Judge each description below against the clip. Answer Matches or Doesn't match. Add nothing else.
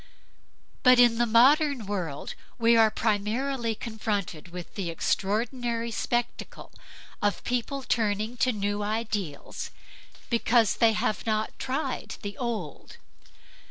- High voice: Matches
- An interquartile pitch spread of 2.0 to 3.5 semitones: Matches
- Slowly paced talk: Matches